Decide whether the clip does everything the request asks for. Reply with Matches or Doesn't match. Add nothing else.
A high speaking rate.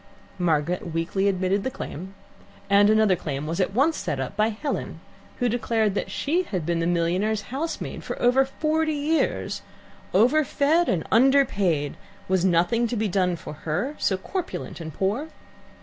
Doesn't match